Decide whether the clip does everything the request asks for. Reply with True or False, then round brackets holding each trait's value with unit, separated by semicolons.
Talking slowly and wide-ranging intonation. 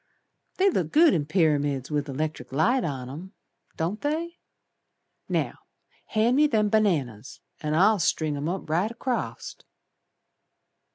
True (130 wpm; 7.2 semitones)